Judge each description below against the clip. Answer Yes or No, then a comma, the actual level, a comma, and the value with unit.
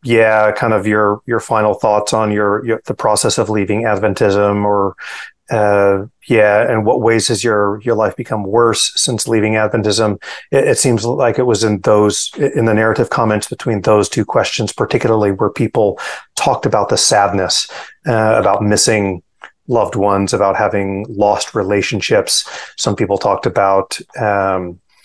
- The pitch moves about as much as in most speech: No, narrow, 1.7 semitones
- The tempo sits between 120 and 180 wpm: Yes, average, 160 wpm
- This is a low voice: Yes, low, 105 Hz